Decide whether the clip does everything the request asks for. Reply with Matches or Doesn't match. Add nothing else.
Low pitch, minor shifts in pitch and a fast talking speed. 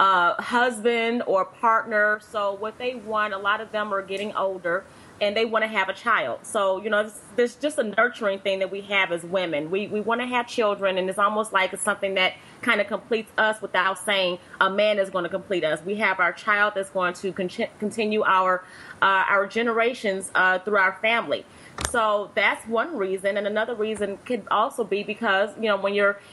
Doesn't match